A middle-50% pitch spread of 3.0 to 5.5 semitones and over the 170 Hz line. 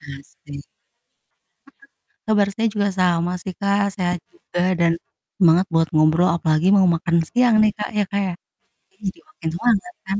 Yes: average, 3.4 semitones; medium, 185 Hz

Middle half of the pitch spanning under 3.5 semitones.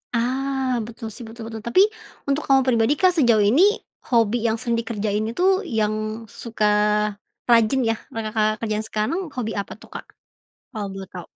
Yes: average, 2.7 semitones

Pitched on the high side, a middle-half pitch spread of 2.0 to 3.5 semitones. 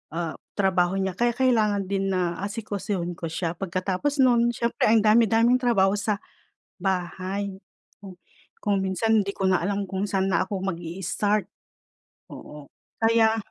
Yes: high, 195 Hz; average, 3.1 semitones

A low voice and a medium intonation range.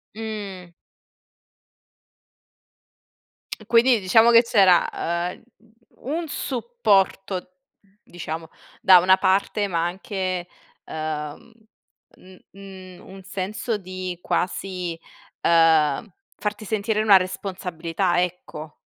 No: medium, 185 Hz; average, 3.0 semitones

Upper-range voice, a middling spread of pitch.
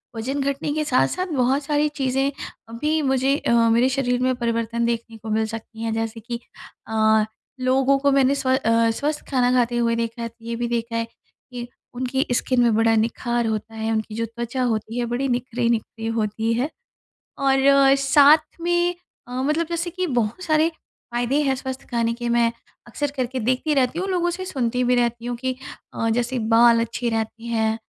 Yes: high, 245 Hz; average, 3.0 semitones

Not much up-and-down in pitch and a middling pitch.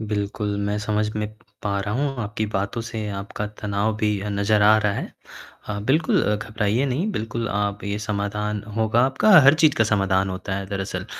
No: narrow, 1.5 semitones; low, 105 Hz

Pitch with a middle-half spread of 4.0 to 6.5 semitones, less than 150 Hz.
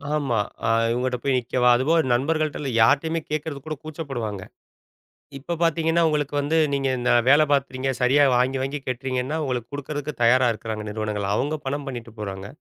No: average, 3.4 semitones; low, 135 Hz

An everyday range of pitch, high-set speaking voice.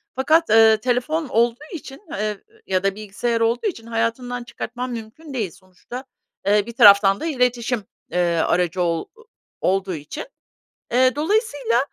Yes: average, 4.3 semitones; high, 230 Hz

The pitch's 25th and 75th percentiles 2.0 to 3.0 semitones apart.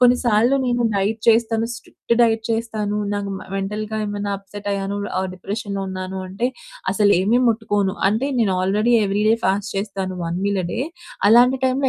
Yes: narrow, 2.6 semitones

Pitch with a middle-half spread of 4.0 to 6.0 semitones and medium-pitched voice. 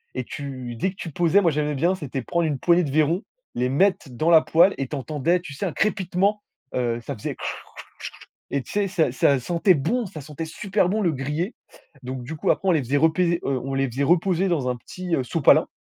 Yes: average, 4.9 semitones; medium, 160 Hz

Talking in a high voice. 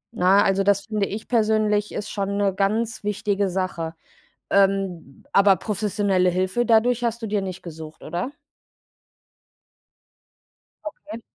Yes: high, 200 Hz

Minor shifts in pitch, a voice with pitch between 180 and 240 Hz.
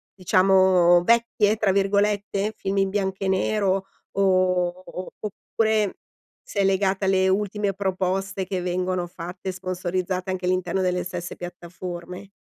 Yes: narrow, 1.4 semitones; high, 190 Hz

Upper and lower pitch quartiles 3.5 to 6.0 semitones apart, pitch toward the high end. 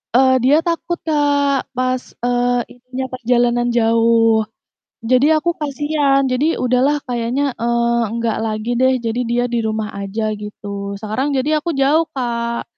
No: average, 2.9 semitones; very high, 250 Hz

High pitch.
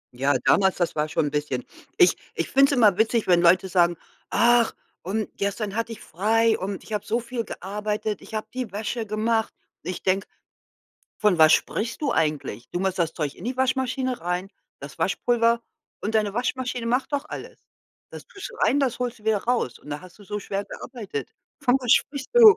Yes: high, 215 Hz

